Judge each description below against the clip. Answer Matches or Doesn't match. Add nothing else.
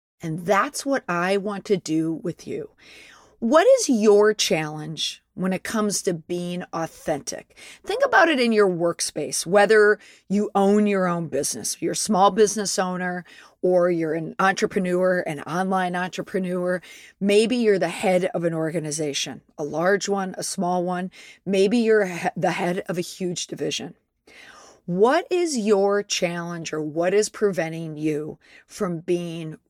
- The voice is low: Doesn't match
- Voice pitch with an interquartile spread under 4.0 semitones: Matches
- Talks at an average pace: Matches